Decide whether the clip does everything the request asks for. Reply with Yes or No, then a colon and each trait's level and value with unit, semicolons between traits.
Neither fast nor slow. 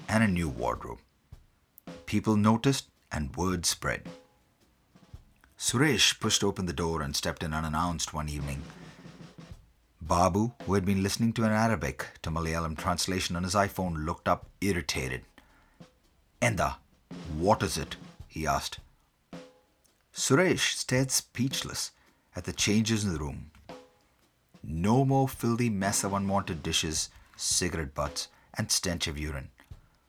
No: slow, 130 wpm